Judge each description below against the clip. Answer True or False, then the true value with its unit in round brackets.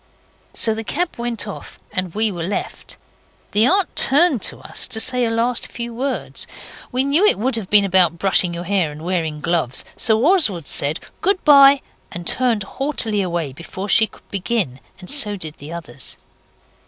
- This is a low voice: False (210 Hz)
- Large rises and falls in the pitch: True (6.4 semitones)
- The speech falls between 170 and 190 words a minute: True (180 wpm)